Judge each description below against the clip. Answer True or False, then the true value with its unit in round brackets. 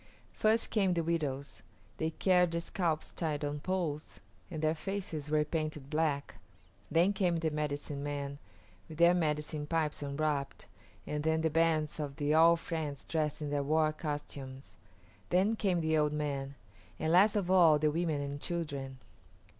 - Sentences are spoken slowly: False (160 wpm)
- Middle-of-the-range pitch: True (155 Hz)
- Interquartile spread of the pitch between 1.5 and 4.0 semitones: True (2.4 semitones)